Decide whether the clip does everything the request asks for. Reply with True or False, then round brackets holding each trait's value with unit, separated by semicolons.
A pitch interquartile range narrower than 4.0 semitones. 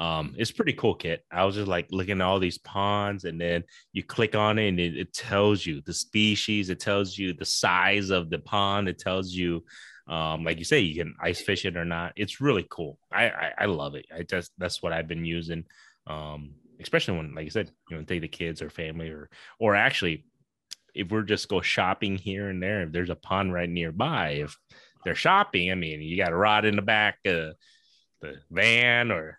True (3.4 semitones)